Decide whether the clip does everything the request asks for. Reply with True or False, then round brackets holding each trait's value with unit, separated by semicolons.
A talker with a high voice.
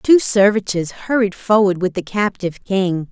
True (195 Hz)